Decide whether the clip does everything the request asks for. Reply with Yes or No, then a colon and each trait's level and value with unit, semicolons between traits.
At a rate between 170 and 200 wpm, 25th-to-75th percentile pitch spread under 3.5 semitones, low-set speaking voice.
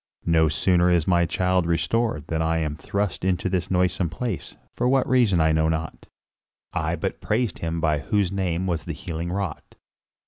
Yes: average, 180 wpm; average, 2.9 semitones; very low, 85 Hz